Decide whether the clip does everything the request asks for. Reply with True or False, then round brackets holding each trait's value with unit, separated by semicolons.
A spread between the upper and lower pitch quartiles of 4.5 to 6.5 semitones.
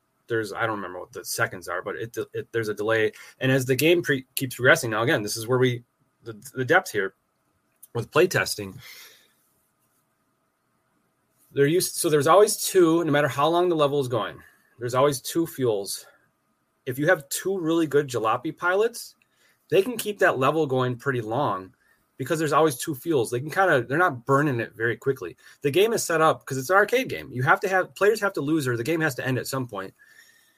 True (5.3 semitones)